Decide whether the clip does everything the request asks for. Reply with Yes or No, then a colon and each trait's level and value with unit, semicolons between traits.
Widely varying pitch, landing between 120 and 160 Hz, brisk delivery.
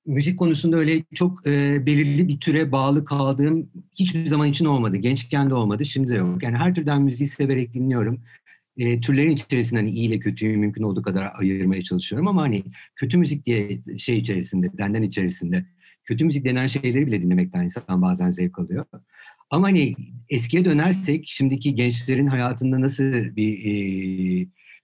Yes: wide, 5.8 semitones; low, 135 Hz; fast, 160 wpm